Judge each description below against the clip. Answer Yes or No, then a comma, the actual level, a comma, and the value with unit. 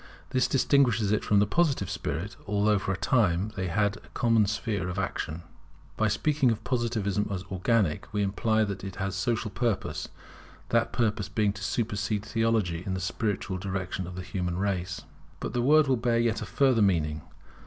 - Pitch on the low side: Yes, low, 105 Hz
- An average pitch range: Yes, average, 3.4 semitones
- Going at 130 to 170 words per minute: No, average, 185 wpm